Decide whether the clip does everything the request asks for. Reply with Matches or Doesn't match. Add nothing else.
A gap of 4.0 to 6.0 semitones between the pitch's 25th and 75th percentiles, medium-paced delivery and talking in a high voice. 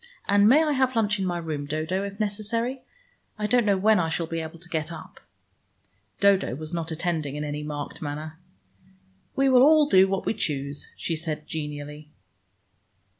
Doesn't match